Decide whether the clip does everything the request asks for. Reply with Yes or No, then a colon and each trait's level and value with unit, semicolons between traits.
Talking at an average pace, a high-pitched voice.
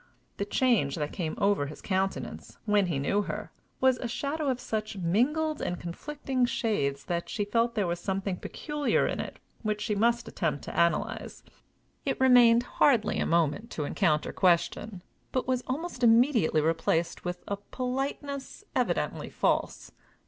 Yes: average, 155 wpm; high, 210 Hz